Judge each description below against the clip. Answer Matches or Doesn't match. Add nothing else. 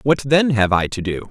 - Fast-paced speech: Matches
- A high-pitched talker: Doesn't match